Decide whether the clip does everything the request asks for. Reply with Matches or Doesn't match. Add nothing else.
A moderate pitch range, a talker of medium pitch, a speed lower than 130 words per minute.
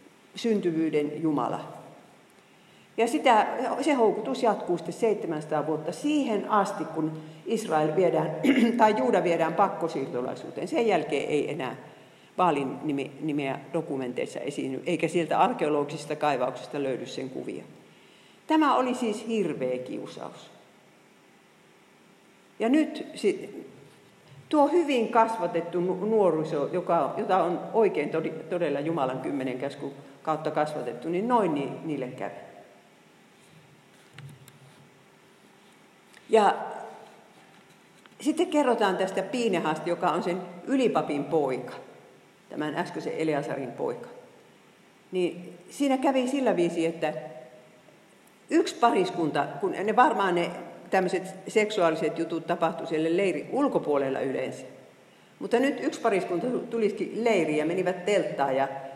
Doesn't match